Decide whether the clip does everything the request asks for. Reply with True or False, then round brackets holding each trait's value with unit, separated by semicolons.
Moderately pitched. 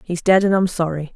True (175 Hz)